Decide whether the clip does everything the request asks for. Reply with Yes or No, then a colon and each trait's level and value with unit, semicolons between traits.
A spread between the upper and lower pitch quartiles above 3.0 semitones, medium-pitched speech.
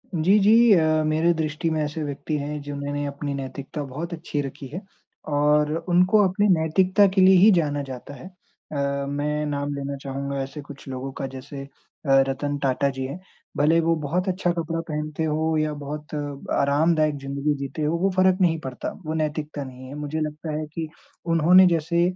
No: average, 2.7 semitones; medium, 150 Hz